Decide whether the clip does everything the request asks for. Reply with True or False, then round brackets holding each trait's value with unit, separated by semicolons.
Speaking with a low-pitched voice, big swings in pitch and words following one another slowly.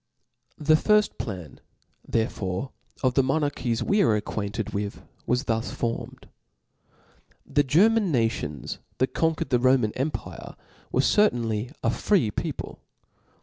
True (125 Hz; 5.8 semitones; 125 wpm)